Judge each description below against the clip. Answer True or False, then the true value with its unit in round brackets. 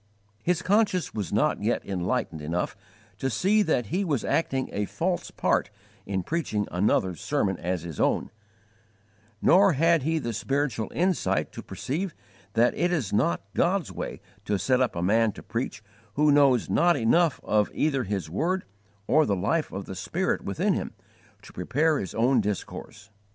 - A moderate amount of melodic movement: False (8.5 semitones)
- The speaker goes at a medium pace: True (165 wpm)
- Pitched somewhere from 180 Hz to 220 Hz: False (130 Hz)